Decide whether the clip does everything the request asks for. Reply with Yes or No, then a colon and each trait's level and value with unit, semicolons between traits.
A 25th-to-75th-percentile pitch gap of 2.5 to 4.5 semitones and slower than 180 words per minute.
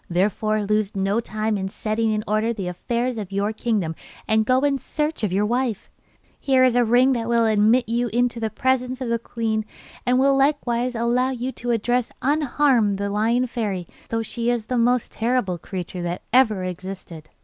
No: average, 3.0 semitones; average, 190 wpm